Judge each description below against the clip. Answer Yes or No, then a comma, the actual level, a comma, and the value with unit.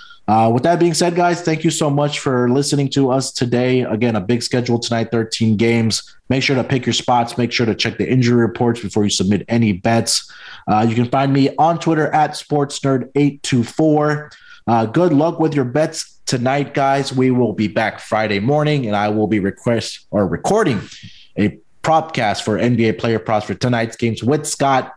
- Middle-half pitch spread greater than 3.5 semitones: Yes, average, 4.2 semitones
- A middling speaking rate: Yes, average, 190 wpm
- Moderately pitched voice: No, low, 125 Hz